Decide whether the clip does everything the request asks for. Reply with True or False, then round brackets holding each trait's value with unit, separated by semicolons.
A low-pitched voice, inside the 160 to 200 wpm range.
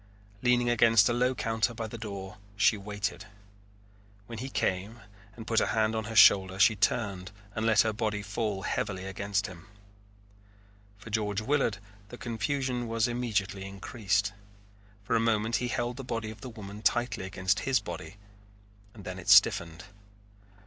True (110 Hz; 165 wpm)